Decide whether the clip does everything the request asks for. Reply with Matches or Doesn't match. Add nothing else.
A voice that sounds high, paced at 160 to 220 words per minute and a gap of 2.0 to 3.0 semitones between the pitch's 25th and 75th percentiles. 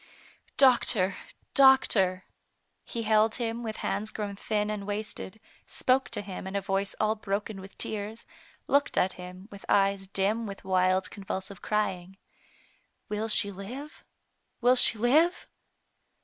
Doesn't match